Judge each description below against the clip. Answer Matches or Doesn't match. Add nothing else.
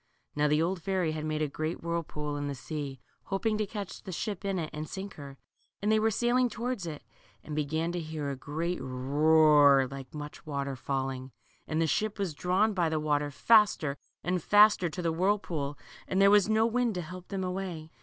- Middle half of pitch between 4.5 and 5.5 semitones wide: Matches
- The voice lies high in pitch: Doesn't match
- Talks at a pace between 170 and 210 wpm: Matches